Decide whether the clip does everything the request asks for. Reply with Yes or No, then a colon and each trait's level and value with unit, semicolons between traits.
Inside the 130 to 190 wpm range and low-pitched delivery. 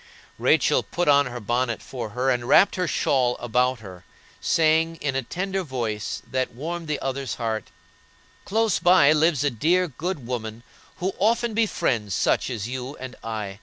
Yes: average, 165 wpm; low, 130 Hz